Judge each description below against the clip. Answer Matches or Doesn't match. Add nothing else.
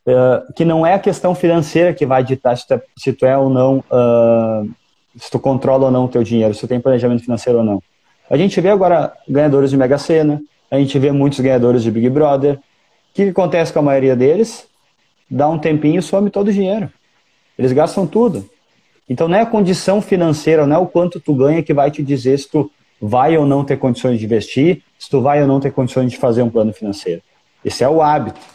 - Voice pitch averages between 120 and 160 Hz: Matches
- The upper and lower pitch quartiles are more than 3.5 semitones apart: Matches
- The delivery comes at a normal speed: Doesn't match